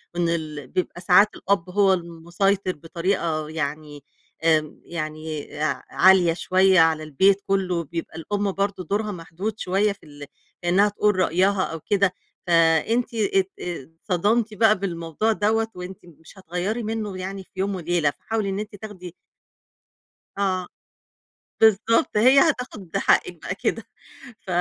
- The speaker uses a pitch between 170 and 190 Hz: Yes, medium, 185 Hz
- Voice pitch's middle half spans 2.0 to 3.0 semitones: No, average, 3.6 semitones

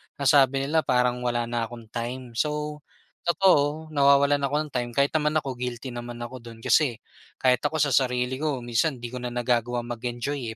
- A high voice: No, low, 125 Hz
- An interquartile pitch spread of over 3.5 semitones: No, average, 3.2 semitones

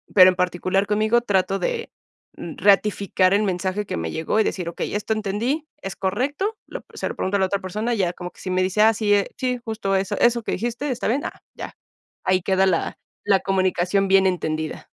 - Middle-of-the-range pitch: No, high, 195 Hz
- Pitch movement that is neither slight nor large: Yes, average, 3.0 semitones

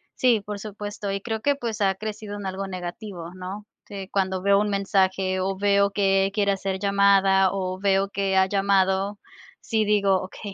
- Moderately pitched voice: No, high, 195 Hz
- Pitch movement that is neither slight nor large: No, narrow, 1.2 semitones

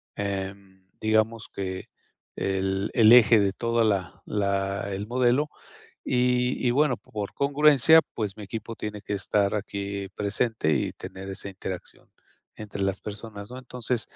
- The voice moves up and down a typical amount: Yes, average, 3.4 semitones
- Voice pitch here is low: Yes, low, 105 Hz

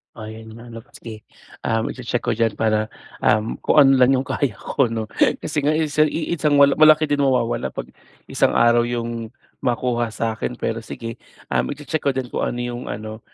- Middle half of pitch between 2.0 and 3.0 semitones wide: No, average, 3.8 semitones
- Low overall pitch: Yes, low, 120 Hz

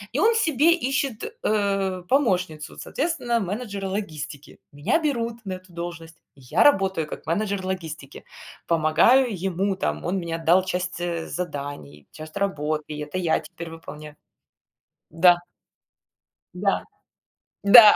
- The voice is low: No, medium, 185 Hz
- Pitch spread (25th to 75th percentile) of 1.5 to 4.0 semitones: No, average, 4.8 semitones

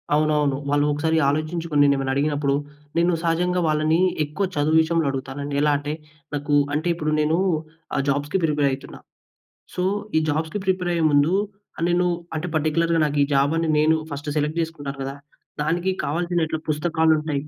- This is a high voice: No, medium, 155 Hz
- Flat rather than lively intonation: Yes, narrow, 2.2 semitones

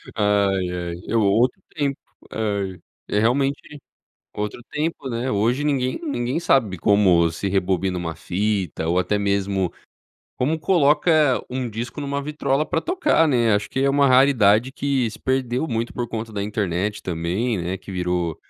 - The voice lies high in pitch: No, low, 110 Hz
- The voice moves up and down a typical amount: No, wide, 5.7 semitones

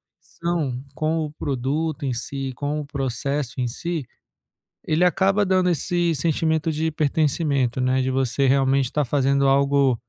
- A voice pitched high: No, medium, 140 Hz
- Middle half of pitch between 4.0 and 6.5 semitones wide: No, average, 3.2 semitones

